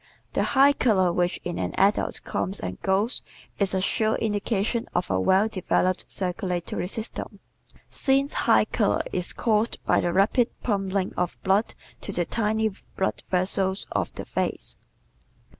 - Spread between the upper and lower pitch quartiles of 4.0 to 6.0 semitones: No, average, 3.1 semitones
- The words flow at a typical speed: Yes, average, 150 wpm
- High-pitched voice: Yes, high, 195 Hz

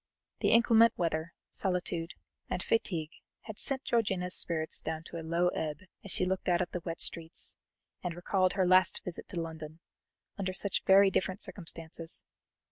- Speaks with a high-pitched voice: No, medium, 180 Hz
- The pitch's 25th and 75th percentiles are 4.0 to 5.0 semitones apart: No, narrow, 2.5 semitones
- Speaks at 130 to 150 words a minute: No, average, 165 wpm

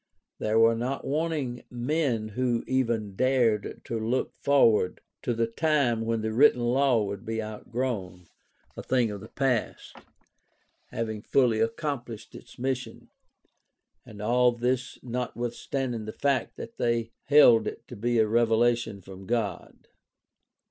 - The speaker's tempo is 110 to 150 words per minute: Yes, average, 140 wpm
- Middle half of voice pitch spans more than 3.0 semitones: No, narrow, 2.6 semitones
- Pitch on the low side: Yes, low, 120 Hz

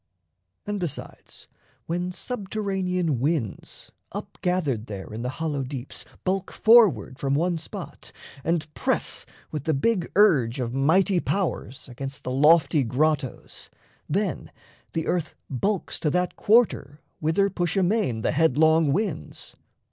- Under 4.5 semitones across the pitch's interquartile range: No, average, 5.3 semitones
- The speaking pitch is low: No, medium, 160 Hz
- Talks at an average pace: No, slow, 130 wpm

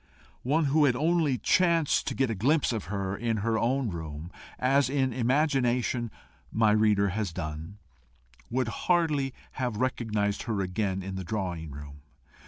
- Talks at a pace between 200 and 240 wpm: No, average, 155 wpm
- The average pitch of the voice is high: No, low, 115 Hz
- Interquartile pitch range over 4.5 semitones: Yes, wide, 5.6 semitones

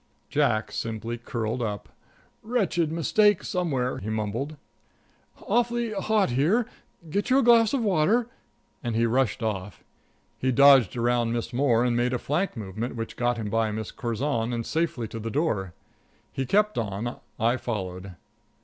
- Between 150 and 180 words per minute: Yes, average, 155 wpm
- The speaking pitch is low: Yes, low, 120 Hz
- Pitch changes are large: Yes, wide, 7.0 semitones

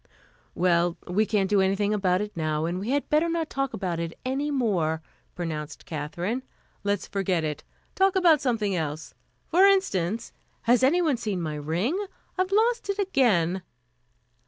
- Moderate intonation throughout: No, wide, 8.8 semitones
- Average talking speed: Yes, average, 160 wpm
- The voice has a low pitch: No, high, 205 Hz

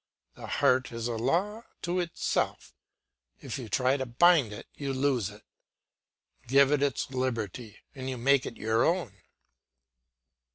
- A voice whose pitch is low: Yes, low, 130 Hz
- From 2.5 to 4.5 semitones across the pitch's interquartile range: Yes, average, 3.4 semitones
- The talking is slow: No, average, 150 wpm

